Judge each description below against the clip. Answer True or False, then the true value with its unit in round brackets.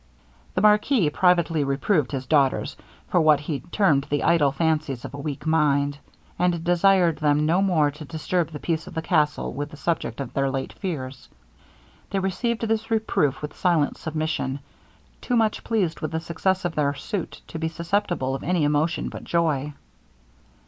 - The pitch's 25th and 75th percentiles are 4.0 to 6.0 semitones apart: False (3.6 semitones)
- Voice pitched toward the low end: False (160 Hz)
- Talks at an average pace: True (175 wpm)